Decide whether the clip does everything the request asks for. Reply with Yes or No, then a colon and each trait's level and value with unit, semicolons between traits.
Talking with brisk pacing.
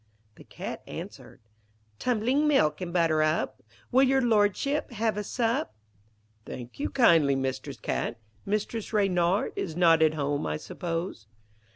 No: average, 140 wpm